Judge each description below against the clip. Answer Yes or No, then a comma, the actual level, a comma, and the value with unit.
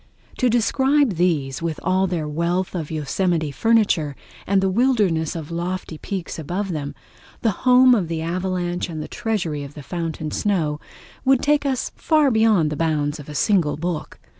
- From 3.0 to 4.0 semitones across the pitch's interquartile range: No, average, 5.2 semitones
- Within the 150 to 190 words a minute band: Yes, average, 165 wpm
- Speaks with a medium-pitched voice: Yes, medium, 175 Hz